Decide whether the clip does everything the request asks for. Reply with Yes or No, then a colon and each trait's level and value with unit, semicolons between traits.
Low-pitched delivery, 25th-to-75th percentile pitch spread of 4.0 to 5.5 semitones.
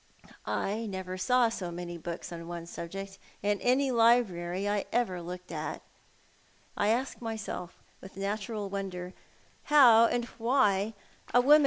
No: high, 200 Hz; average, 4.4 semitones